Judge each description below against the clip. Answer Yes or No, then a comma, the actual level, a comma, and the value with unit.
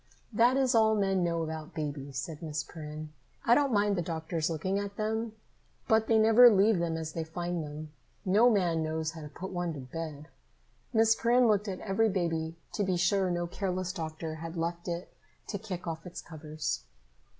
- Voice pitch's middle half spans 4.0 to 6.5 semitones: Yes, average, 4.4 semitones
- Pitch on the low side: No, medium, 175 Hz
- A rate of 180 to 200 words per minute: Yes, average, 195 wpm